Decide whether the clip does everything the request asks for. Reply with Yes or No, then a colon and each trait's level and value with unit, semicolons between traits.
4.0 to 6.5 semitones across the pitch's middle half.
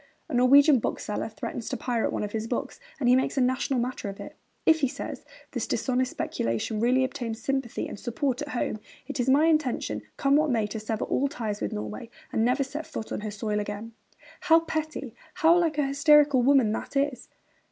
Yes: average, 4.4 semitones